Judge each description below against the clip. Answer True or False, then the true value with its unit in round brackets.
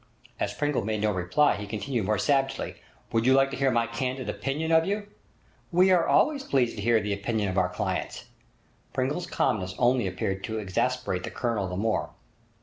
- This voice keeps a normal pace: True (190 wpm)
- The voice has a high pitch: False (120 Hz)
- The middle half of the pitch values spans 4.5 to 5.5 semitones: True (4.9 semitones)